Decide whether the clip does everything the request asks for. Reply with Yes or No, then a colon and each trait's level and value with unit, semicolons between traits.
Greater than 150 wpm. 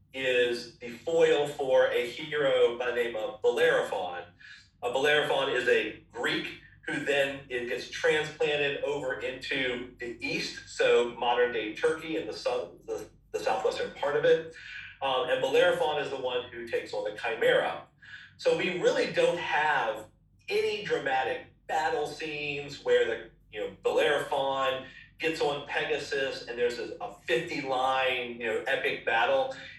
No: average, 145 wpm